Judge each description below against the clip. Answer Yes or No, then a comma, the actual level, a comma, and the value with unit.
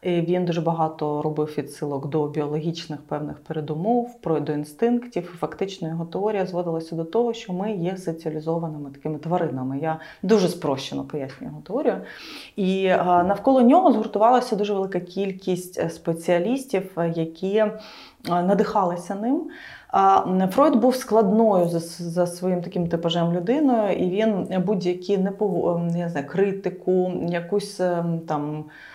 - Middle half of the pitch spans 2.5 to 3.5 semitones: No, average, 3.9 semitones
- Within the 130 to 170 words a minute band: No, average, 120 wpm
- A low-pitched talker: No, medium, 180 Hz